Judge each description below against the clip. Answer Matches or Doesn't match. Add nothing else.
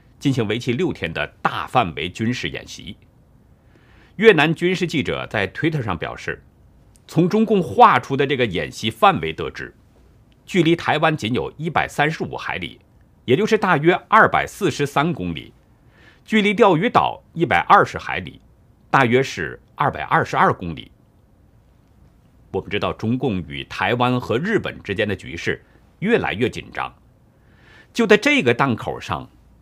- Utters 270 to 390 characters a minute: Doesn't match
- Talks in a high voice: Doesn't match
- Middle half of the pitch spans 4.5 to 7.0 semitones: Doesn't match